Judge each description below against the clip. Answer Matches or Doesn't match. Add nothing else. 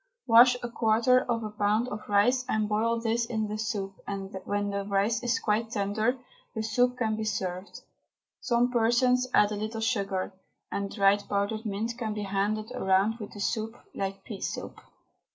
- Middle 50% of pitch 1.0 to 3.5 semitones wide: Matches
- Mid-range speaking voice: Doesn't match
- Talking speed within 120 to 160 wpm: Doesn't match